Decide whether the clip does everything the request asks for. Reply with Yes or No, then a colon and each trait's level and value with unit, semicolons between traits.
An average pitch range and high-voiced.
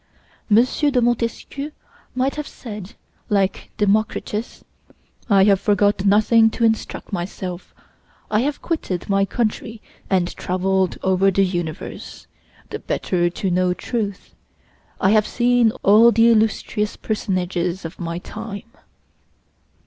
Yes: average, 3.4 semitones; high, 205 Hz